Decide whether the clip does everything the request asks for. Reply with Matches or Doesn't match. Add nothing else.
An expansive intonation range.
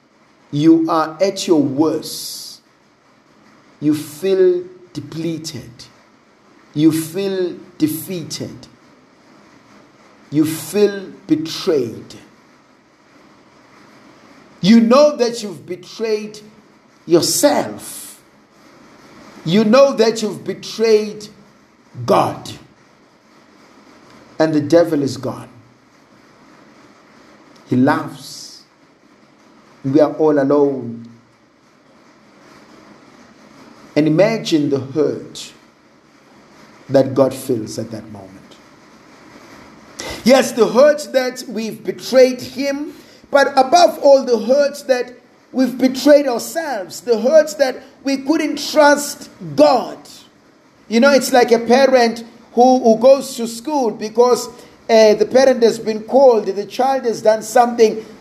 Matches